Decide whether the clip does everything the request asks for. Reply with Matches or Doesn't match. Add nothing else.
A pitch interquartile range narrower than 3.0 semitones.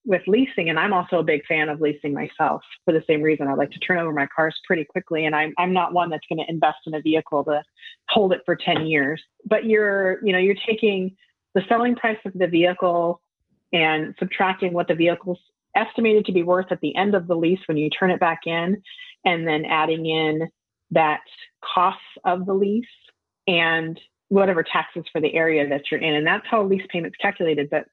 Doesn't match